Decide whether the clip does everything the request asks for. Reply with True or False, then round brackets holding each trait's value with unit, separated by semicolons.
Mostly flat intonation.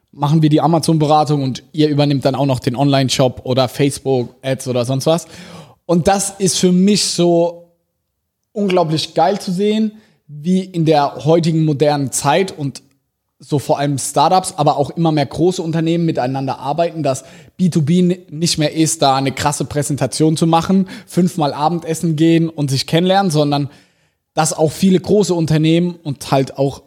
False (3.5 semitones)